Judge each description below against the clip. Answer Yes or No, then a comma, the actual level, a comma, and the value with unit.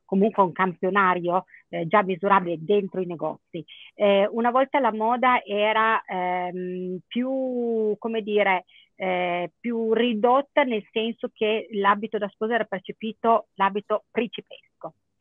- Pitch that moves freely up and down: No, average, 3.4 semitones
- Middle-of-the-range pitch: No, high, 210 Hz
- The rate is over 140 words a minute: No, average, 125 wpm